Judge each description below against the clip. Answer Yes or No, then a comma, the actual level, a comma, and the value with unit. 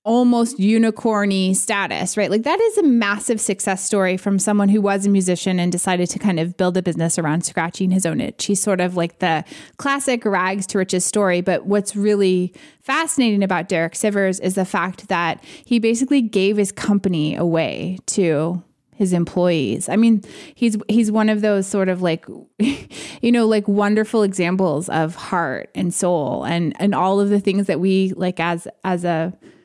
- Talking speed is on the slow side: No, average, 185 wpm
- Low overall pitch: No, high, 195 Hz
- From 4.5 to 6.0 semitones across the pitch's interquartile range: No, average, 2.9 semitones